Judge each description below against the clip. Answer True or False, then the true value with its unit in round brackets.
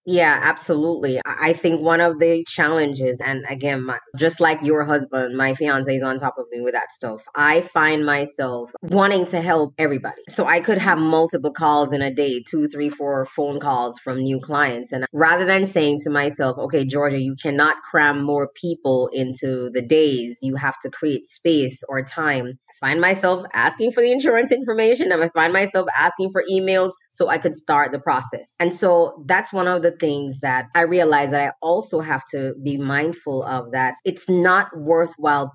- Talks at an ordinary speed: True (190 wpm)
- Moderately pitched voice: True (150 Hz)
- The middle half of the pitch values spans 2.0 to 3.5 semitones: False (3.9 semitones)